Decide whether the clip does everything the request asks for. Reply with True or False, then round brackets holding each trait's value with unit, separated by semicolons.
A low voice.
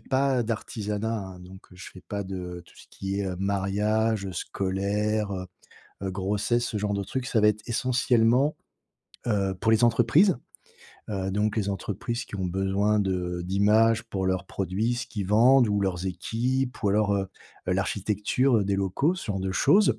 True (105 Hz)